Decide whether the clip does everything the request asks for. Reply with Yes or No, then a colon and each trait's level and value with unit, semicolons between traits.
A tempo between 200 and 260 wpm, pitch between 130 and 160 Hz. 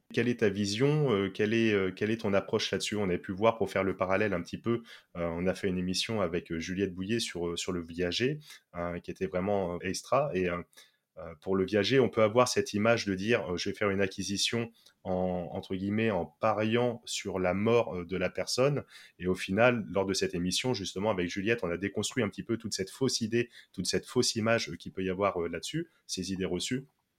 No: average, 215 wpm; low, 100 Hz